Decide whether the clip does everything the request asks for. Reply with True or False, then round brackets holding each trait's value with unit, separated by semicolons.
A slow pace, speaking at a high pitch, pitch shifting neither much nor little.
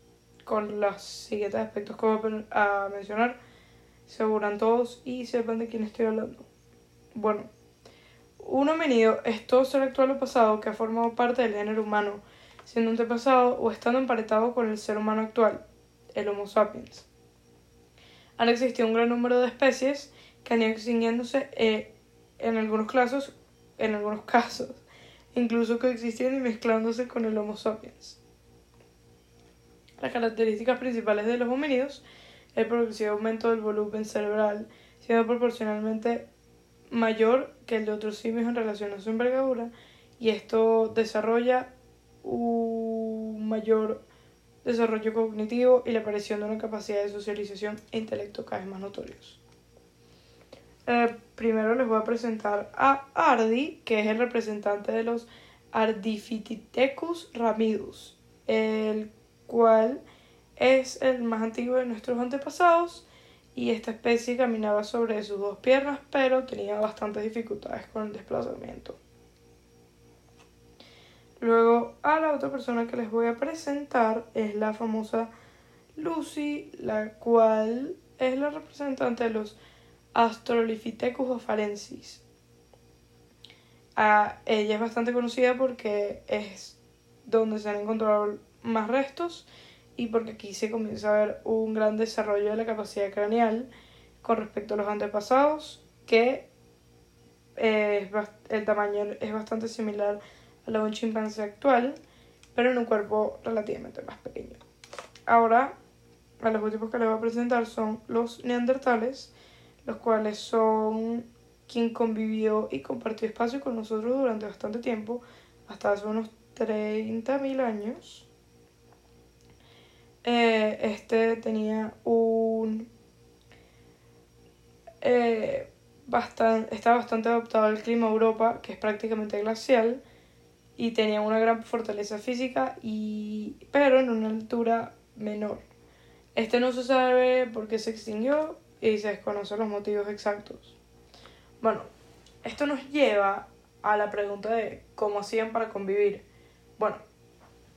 False (125 wpm; 225 Hz; 2.1 semitones)